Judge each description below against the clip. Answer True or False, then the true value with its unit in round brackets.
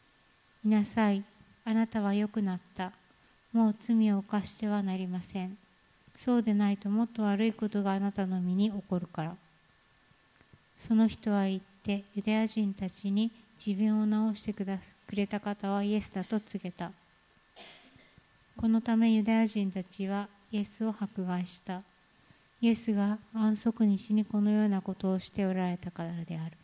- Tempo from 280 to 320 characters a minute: True (295 characters per minute)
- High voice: True (205 Hz)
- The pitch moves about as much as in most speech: False (2.2 semitones)